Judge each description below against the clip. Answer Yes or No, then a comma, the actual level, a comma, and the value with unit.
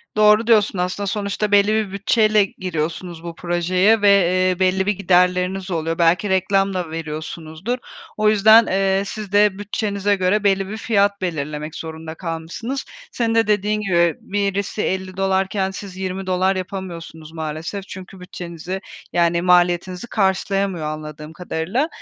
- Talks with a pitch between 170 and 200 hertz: Yes, high, 190 Hz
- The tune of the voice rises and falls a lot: No, average, 2.9 semitones